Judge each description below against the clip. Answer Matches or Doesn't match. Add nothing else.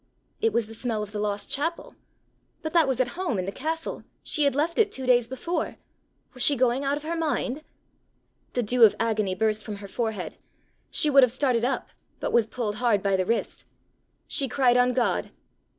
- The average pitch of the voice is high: Matches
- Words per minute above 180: Matches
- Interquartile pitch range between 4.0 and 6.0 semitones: Matches